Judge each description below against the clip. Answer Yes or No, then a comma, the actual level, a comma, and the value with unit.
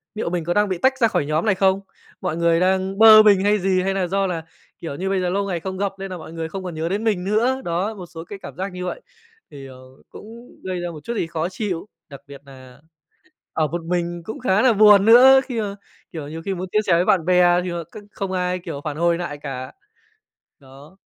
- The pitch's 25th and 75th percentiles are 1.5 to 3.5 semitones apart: Yes, average, 3.1 semitones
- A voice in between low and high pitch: Yes, medium, 180 Hz